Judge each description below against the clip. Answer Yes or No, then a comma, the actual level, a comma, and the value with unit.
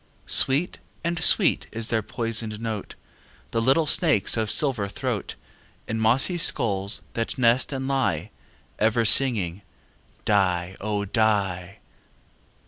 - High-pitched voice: No, low, 115 Hz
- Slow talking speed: Yes, slow, 120 wpm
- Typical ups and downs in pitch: Yes, average, 4.4 semitones